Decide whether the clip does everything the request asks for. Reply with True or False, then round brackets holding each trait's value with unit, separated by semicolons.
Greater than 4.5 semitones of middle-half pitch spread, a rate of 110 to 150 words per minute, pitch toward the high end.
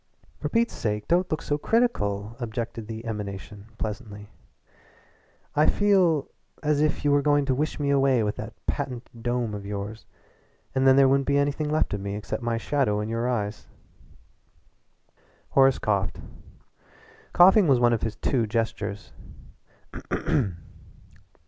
False (5.4 semitones; 145 wpm; 120 Hz)